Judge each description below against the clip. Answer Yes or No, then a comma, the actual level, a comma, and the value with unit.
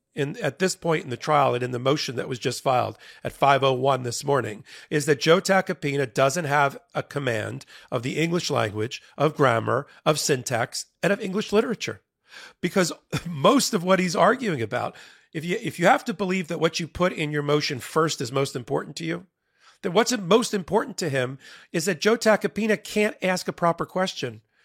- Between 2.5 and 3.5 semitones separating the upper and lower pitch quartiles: No, wide, 5.6 semitones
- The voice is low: No, medium, 160 Hz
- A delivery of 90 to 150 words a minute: No, average, 195 wpm